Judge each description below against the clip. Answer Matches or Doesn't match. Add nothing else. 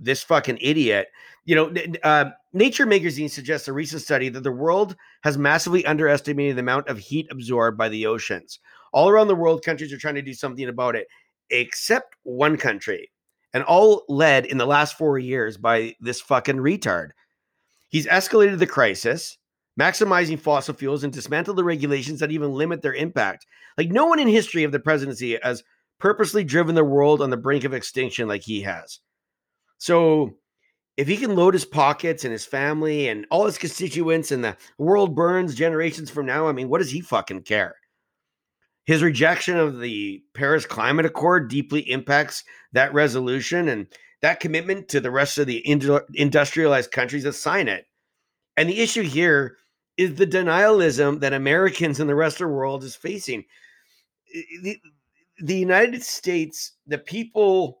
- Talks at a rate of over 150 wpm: Matches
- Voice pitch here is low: Doesn't match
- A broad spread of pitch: Doesn't match